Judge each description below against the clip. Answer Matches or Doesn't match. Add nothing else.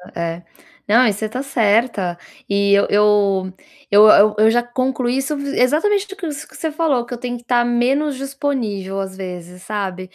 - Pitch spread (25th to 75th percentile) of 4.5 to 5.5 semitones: Matches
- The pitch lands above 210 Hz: Matches